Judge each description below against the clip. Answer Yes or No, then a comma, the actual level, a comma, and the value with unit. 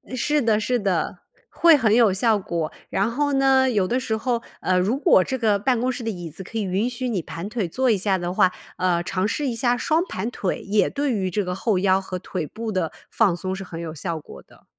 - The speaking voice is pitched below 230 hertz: Yes, high, 210 Hz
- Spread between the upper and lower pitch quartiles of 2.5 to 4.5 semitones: No, average, 4.9 semitones